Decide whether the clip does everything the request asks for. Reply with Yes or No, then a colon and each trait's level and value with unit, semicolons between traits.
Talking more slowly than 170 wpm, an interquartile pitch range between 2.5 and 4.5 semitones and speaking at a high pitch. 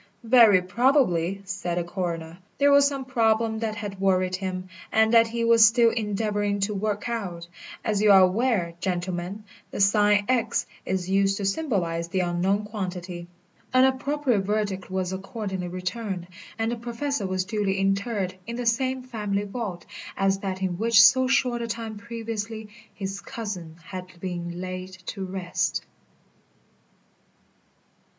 Yes: average, 150 wpm; average, 3.7 semitones; high, 200 Hz